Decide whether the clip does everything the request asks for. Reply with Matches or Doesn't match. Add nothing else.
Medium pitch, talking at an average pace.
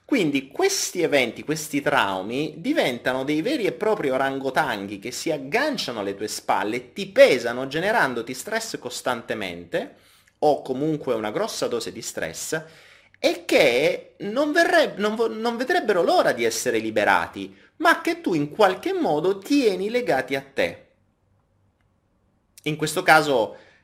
Matches